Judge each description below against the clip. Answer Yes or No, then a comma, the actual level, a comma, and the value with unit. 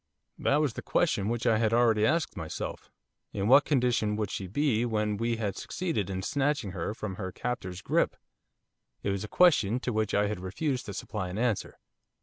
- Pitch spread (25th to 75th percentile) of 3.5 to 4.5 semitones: Yes, average, 3.9 semitones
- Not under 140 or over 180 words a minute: No, average, 195 wpm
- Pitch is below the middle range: Yes, low, 110 Hz